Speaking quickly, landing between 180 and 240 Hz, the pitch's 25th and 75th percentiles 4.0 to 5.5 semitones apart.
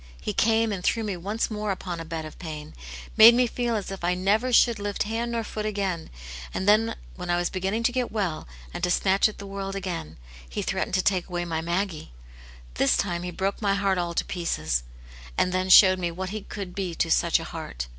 No: fast, 235 wpm; high, 190 Hz; average, 3.4 semitones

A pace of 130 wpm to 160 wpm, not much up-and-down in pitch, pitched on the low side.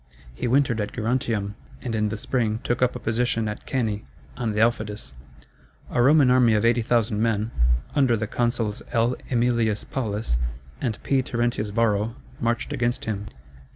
Yes: average, 155 wpm; narrow, 2.3 semitones; low, 115 Hz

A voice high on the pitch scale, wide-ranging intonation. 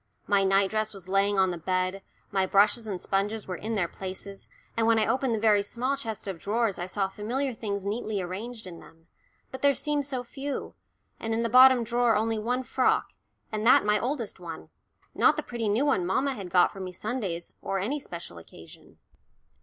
No: high, 210 Hz; average, 3.9 semitones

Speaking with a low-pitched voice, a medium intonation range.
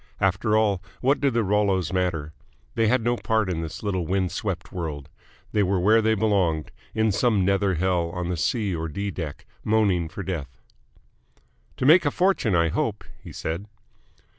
Yes: very low, 95 Hz; average, 4.0 semitones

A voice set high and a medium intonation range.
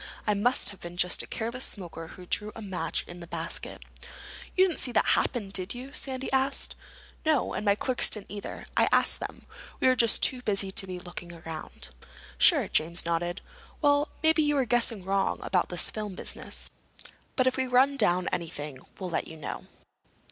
No: high, 205 Hz; wide, 6.4 semitones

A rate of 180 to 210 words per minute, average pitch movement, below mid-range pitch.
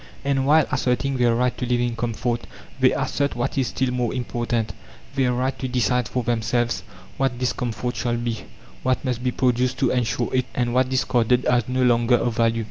No: average, 200 wpm; narrow, 1.3 semitones; low, 125 Hz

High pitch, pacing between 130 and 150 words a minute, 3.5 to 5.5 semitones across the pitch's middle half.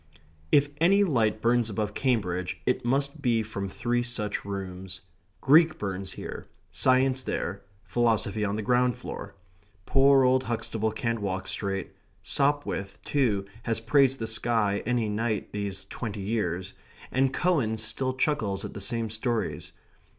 No: low, 115 Hz; average, 145 wpm; average, 4.3 semitones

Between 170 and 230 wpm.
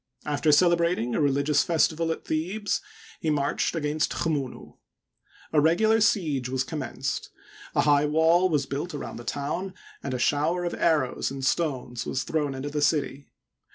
No: average, 155 wpm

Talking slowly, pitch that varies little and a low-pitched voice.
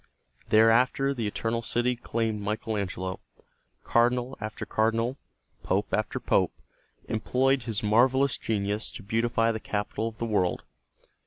Yes: slow, 130 wpm; narrow, 2.2 semitones; low, 115 Hz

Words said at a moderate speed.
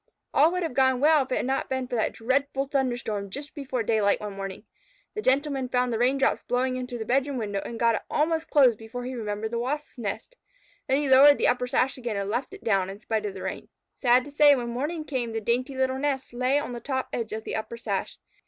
No: fast, 245 wpm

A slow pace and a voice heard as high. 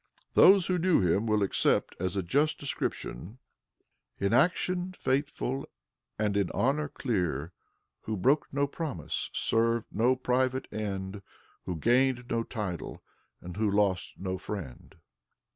No: slow, 130 wpm; low, 115 Hz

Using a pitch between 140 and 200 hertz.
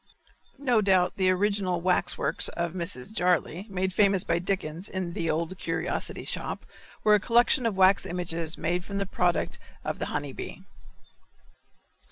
Yes: medium, 185 Hz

